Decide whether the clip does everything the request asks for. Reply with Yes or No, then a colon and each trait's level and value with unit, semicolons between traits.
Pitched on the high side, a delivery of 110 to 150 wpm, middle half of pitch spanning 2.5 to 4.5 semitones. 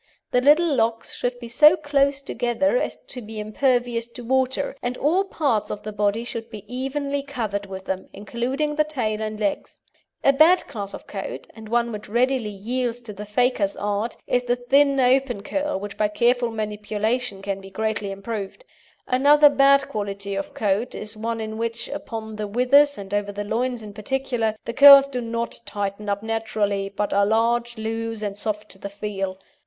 No: high, 230 Hz; average, 185 wpm; average, 3.7 semitones